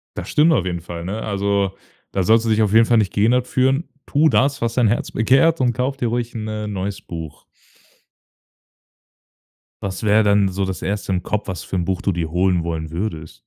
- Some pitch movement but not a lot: Yes, average, 4.1 semitones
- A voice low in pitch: Yes, low, 105 Hz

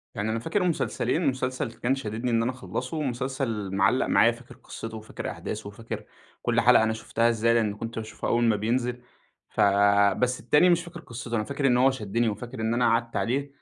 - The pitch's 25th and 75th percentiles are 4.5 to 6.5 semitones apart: No, narrow, 2.6 semitones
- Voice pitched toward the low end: Yes, low, 120 Hz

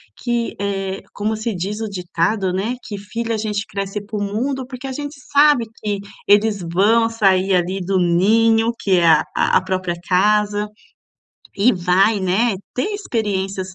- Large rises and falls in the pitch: No, average, 3.1 semitones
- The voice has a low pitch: No, high, 205 Hz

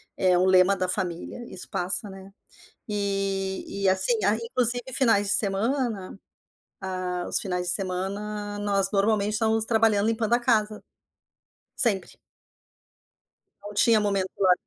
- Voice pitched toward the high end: Yes, high, 200 Hz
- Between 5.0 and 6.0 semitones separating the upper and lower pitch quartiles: No, narrow, 2.5 semitones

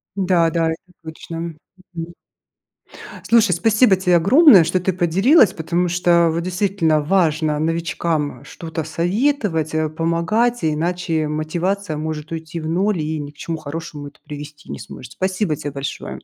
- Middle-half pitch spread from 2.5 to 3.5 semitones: Yes, average, 3.0 semitones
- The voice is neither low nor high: Yes, medium, 165 Hz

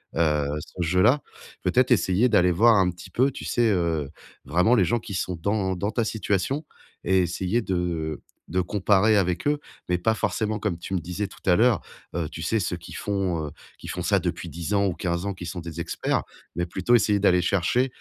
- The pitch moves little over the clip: No, average, 3.7 semitones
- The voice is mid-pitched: No, very low, 95 Hz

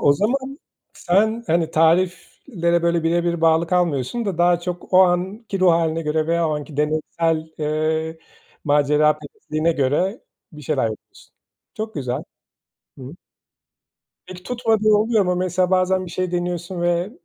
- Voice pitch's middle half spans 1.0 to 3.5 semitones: Yes, average, 2.8 semitones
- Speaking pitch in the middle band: Yes, medium, 170 Hz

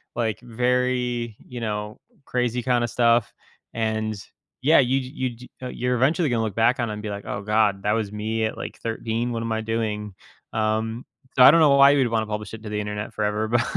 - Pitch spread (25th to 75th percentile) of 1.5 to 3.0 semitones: Yes, narrow, 2.4 semitones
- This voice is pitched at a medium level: No, low, 115 Hz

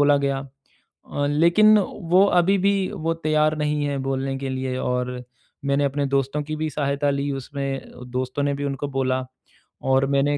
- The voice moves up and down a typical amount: No, narrow, 2.0 semitones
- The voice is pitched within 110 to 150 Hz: Yes, medium, 140 Hz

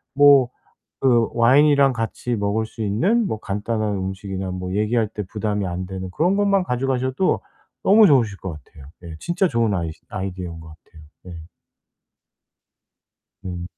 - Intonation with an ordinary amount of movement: No, wide, 5.8 semitones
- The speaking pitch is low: Yes, low, 110 Hz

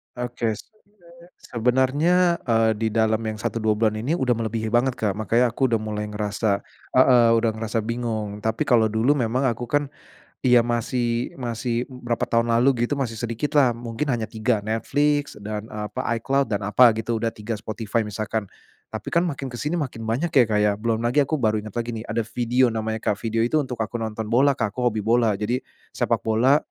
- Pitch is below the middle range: Yes, low, 115 Hz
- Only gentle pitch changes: Yes, narrow, 2.3 semitones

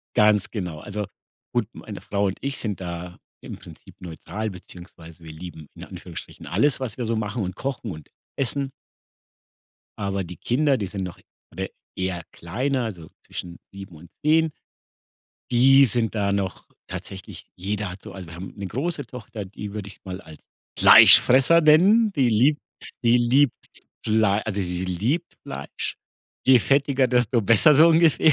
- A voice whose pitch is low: Yes, low, 105 Hz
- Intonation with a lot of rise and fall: Yes, wide, 6.0 semitones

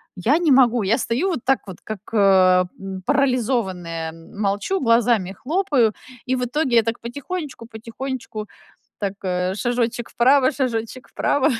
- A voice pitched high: Yes, high, 235 Hz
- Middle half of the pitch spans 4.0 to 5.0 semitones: Yes, average, 4.4 semitones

